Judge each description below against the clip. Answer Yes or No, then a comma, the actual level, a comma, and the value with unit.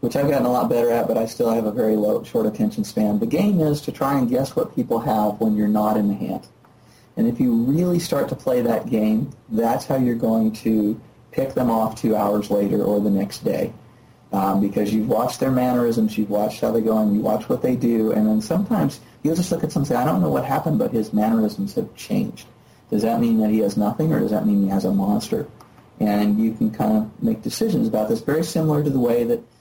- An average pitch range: No, wide, 7.2 semitones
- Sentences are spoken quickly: Yes, fast, 250 wpm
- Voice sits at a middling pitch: No, low, 115 Hz